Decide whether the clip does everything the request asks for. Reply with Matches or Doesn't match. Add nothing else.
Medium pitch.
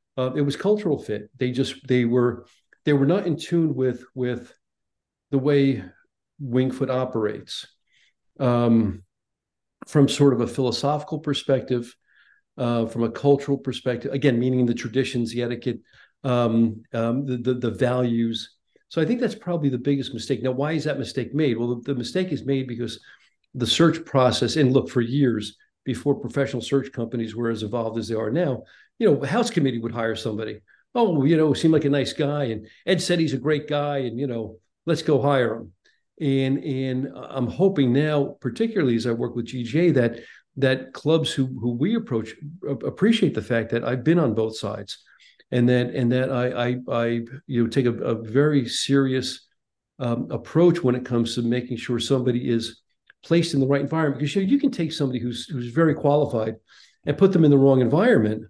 Doesn't match